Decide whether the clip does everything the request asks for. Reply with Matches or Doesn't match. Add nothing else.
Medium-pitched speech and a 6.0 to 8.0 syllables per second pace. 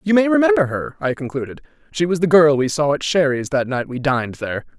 Matches